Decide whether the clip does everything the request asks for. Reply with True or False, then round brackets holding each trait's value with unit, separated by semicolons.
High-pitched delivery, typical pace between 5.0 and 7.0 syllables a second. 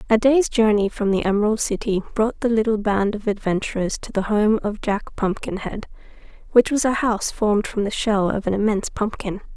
True (210 Hz; 5.5 syllables/s)